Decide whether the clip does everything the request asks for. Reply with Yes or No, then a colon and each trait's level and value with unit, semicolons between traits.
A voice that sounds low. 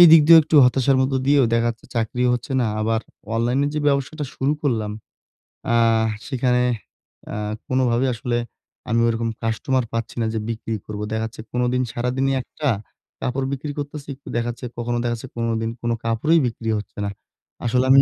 Yes: low, 125 Hz